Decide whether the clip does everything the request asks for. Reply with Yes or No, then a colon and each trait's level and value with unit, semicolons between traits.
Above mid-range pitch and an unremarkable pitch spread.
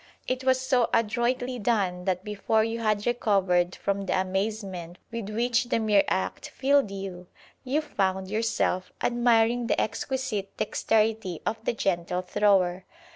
Yes: high, 215 Hz; average, 3.9 semitones